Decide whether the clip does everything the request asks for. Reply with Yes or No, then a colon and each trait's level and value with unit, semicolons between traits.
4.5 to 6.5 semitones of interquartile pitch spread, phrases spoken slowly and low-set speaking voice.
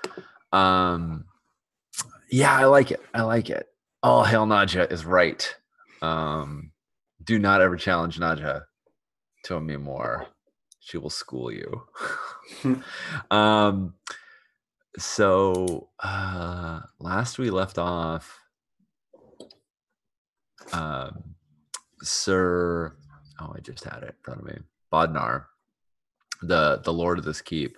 No: average, 3.6 semitones; slow, 110 wpm; very low, 90 Hz